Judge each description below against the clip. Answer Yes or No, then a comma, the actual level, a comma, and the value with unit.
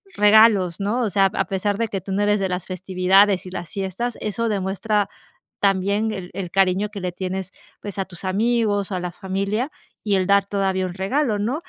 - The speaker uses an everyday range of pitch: No, narrow, 1.9 semitones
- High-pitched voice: Yes, high, 195 Hz